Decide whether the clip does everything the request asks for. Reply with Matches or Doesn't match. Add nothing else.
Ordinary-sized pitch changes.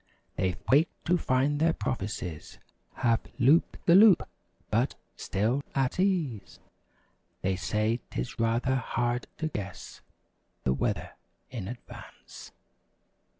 Doesn't match